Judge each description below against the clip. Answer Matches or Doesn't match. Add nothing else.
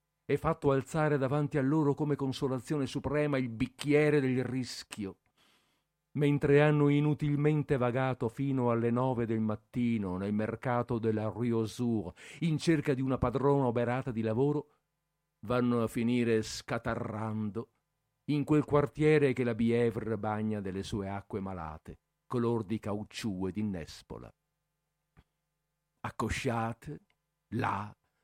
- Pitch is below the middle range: Matches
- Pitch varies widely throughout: Doesn't match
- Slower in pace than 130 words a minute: Matches